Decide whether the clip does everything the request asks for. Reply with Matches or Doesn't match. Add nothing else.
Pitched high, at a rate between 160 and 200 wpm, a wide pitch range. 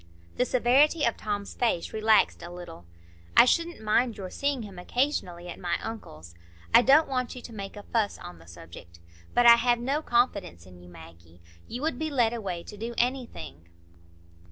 Matches